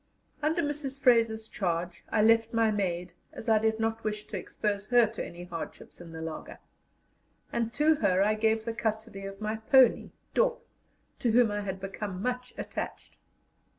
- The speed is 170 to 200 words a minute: Yes, average, 175 wpm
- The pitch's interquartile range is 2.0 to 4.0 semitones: Yes, average, 3.1 semitones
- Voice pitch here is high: Yes, high, 220 Hz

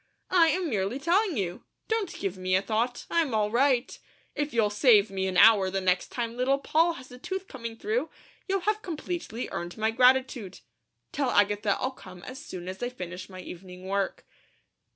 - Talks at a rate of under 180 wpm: No, average, 190 wpm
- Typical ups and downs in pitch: No, wide, 6.8 semitones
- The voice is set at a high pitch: Yes, high, 235 Hz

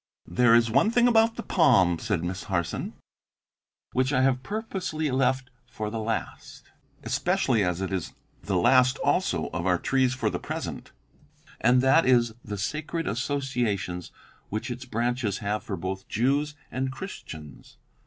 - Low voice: Yes, low, 125 Hz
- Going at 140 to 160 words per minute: Yes, average, 155 wpm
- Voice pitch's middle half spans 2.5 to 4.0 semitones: No, average, 5.2 semitones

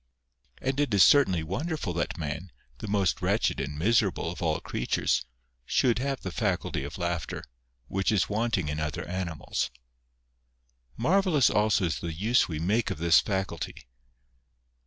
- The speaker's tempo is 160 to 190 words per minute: No, average, 150 wpm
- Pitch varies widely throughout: Yes, wide, 6.0 semitones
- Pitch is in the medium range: No, very low, 95 Hz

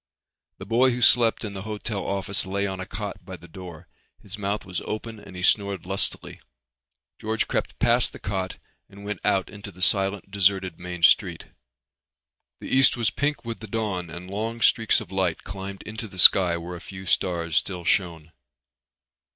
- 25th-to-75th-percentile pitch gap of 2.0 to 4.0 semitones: Yes, average, 2.8 semitones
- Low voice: Yes, very low, 95 Hz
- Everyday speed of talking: Yes, average, 185 wpm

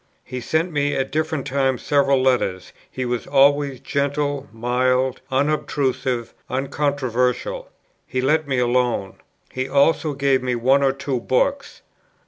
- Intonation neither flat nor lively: No, narrow, 2.0 semitones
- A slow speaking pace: Yes, slow, 130 wpm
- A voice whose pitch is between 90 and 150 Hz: Yes, low, 135 Hz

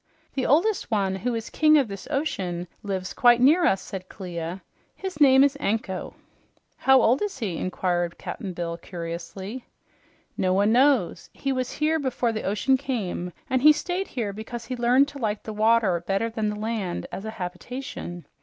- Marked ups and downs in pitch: Yes, wide, 5.9 semitones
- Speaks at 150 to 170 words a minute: No, average, 180 wpm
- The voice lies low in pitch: No, high, 220 Hz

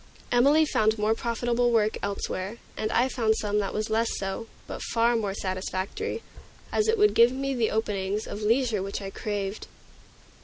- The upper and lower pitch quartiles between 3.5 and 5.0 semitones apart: No, average, 3.0 semitones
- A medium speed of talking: Yes, average, 170 wpm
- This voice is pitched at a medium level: No, high, 220 Hz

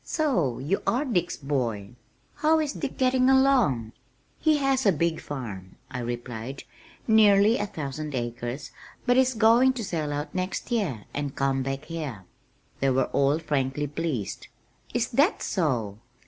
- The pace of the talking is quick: No, average, 150 wpm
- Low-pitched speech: No, medium, 150 Hz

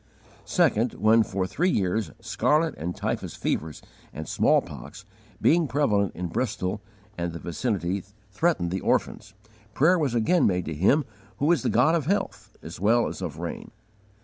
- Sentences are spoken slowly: No, average, 160 wpm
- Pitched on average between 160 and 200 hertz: No, low, 105 Hz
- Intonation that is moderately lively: No, wide, 8.2 semitones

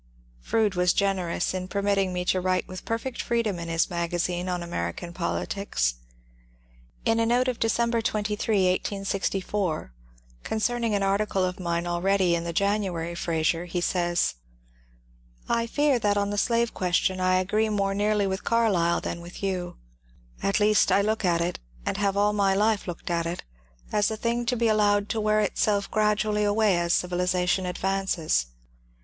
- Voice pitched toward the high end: Yes, high, 195 Hz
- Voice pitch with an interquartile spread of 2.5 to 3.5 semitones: Yes, average, 3.2 semitones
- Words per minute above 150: Yes, average, 170 wpm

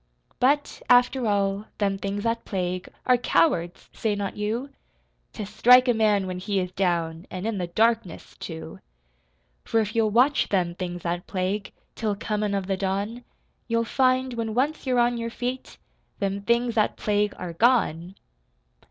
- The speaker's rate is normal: Yes, average, 165 wpm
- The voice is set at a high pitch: Yes, high, 210 Hz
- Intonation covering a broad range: No, average, 3.9 semitones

